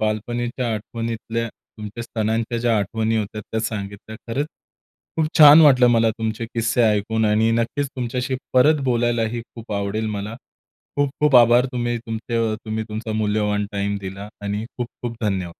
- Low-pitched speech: Yes, low, 115 Hz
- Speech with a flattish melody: Yes, narrow, 2.0 semitones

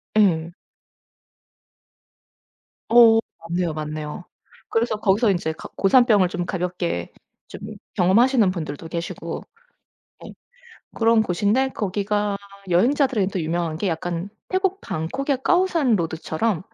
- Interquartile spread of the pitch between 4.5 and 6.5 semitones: Yes, average, 5.2 semitones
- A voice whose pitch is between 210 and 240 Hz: No, high, 195 Hz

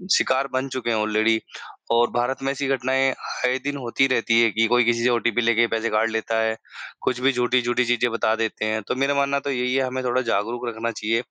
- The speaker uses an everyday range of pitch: No, narrow, 2.3 semitones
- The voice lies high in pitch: No, low, 120 Hz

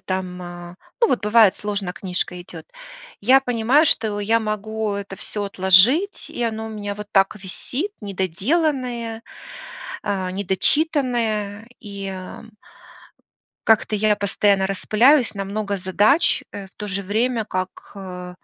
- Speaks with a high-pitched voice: Yes, high, 205 Hz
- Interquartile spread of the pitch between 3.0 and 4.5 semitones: No, narrow, 2.6 semitones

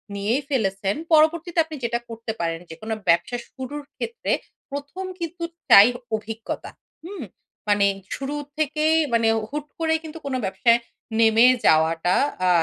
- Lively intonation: Yes, wide, 7.1 semitones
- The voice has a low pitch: No, high, 245 Hz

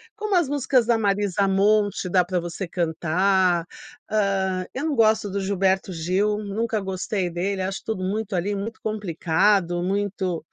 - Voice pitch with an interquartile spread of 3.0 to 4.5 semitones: No, narrow, 2.5 semitones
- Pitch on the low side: No, high, 195 Hz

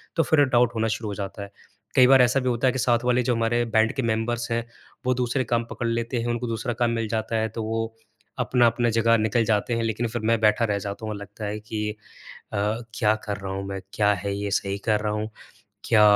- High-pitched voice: No, low, 115 Hz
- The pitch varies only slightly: Yes, narrow, 2.1 semitones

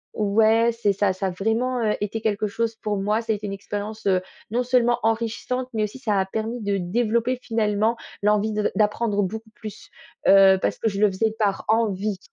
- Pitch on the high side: Yes, high, 215 Hz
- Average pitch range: No, narrow, 2.0 semitones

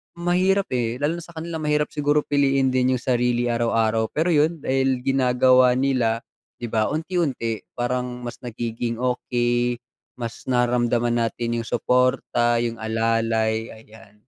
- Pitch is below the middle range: Yes, low, 125 Hz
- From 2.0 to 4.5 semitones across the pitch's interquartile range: Yes, average, 2.7 semitones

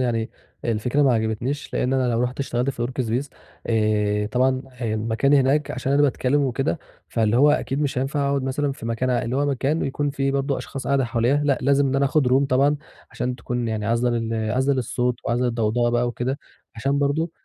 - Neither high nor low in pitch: No, low, 130 Hz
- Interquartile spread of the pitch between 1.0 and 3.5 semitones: Yes, average, 2.8 semitones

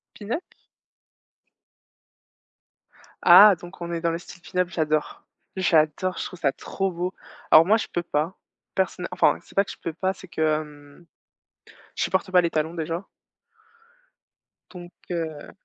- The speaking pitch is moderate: Yes, medium, 175 Hz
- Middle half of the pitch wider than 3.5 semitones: No, average, 2.8 semitones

